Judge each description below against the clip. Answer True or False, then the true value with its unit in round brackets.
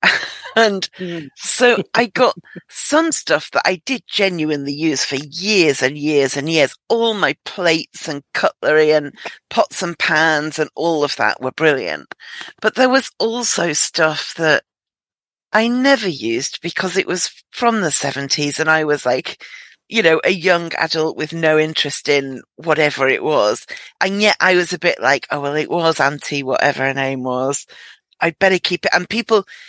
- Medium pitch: True (160 Hz)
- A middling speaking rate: True (170 wpm)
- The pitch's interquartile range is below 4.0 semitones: False (5.0 semitones)